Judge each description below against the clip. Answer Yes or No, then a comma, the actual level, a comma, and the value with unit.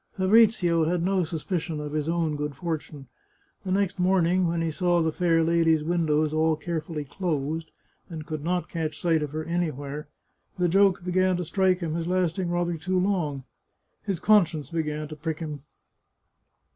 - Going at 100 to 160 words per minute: No, average, 170 wpm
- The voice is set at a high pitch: No, medium, 165 Hz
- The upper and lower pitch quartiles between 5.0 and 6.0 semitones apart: No, narrow, 2.6 semitones